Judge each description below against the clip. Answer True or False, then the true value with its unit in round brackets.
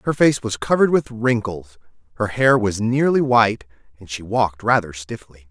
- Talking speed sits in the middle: True (175 wpm)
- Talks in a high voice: False (110 Hz)